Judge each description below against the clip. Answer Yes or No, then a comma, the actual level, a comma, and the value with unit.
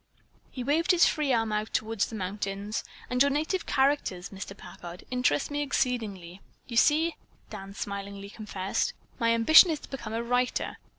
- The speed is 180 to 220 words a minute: No, average, 165 wpm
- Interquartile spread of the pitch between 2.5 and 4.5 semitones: No, wide, 5.6 semitones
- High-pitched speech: Yes, high, 225 Hz